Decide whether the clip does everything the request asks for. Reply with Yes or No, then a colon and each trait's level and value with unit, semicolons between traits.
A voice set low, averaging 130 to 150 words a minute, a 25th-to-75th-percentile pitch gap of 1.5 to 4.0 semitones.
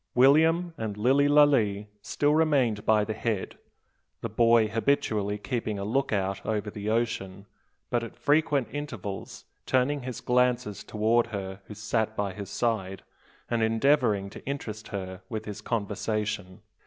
Yes: low, 110 Hz; average, 140 wpm; average, 3.6 semitones